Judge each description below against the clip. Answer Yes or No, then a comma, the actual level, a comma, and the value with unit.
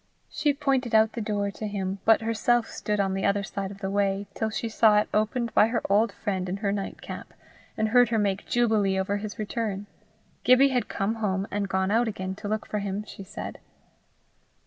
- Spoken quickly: Yes, fast, 215 wpm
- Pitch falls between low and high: No, high, 210 Hz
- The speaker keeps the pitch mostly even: Yes, narrow, 2.3 semitones